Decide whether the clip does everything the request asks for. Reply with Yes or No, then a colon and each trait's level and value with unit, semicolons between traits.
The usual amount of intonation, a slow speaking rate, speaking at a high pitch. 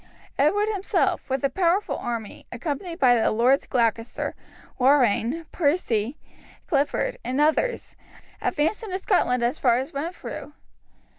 No: wide, 6.1 semitones; slow, 125 wpm; very high, 280 Hz